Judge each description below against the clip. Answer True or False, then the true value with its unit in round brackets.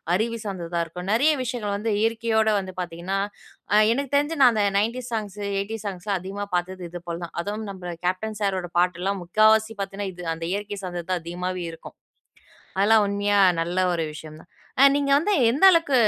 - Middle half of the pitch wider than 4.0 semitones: False (3.7 semitones)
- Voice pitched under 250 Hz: True (200 Hz)